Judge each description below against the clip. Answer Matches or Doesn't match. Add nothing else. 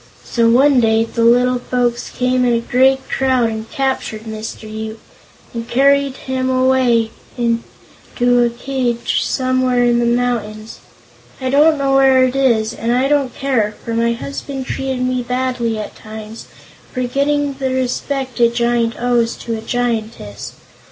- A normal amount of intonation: Doesn't match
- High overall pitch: Matches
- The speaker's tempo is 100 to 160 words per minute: Matches